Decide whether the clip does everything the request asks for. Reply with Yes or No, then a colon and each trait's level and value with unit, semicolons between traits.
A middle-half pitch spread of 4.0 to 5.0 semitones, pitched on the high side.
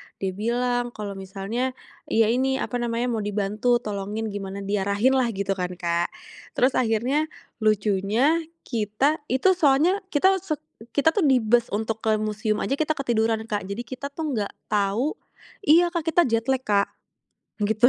Yes: average, 4.5 semitones; high, 230 Hz